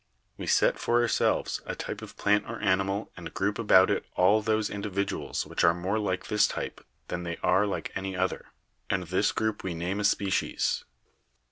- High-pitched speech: No, low, 100 Hz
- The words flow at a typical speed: Yes, average, 190 wpm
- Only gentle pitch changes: Yes, narrow, 2.1 semitones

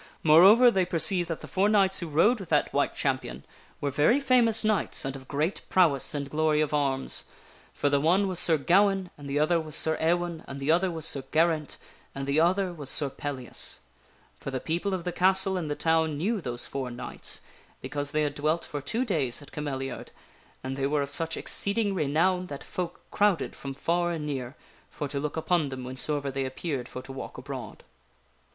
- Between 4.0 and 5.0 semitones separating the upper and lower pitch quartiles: Yes, average, 4.4 semitones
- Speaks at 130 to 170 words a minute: No, fast, 205 wpm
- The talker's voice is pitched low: No, medium, 155 Hz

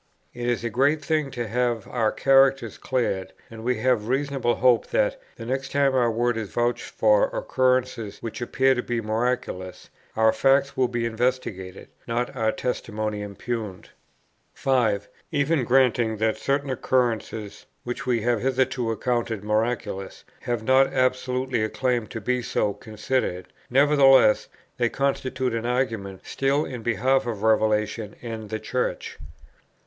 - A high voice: No, low, 120 Hz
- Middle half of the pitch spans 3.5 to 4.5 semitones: No, average, 3.0 semitones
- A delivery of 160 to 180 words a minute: No, average, 145 wpm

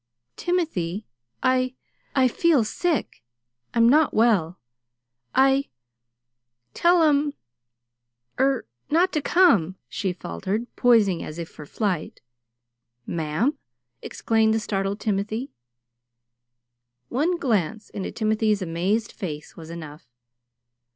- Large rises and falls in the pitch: Yes, wide, 6.7 semitones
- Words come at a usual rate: No, slow, 100 wpm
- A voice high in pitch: Yes, high, 220 Hz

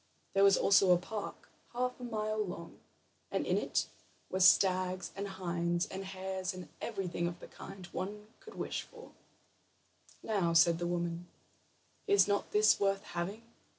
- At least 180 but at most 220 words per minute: No, average, 155 wpm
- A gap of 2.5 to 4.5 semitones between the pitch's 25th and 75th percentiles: Yes, average, 3.0 semitones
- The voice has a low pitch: No, high, 190 Hz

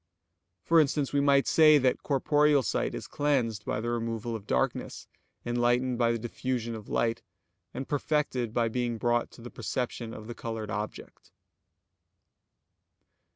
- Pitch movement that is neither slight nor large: Yes, average, 3.3 semitones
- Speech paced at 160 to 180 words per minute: No, average, 150 wpm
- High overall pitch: No, low, 120 Hz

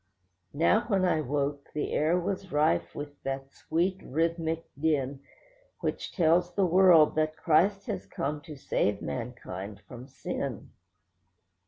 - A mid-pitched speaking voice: Yes, medium, 155 Hz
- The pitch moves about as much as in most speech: Yes, average, 4.2 semitones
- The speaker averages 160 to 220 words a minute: No, slow, 135 wpm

